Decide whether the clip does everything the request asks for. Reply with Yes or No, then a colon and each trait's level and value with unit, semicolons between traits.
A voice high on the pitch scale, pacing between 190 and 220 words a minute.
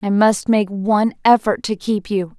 Yes: high, 205 Hz; average, 200 wpm